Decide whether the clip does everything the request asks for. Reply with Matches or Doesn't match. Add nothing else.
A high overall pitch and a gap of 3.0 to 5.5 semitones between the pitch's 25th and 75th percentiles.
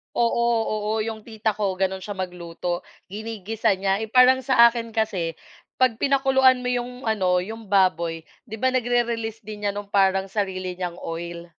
Matches